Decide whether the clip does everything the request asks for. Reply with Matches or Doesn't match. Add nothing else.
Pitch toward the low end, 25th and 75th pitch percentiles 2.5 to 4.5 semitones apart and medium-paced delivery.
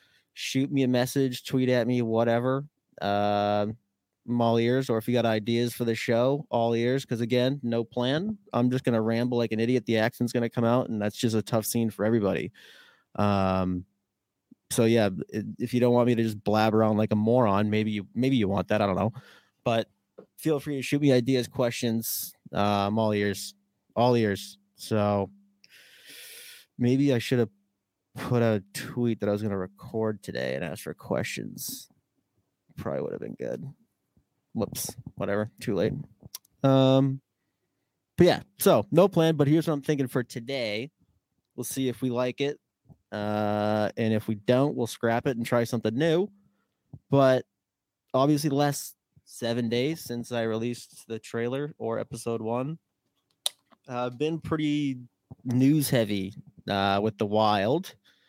Matches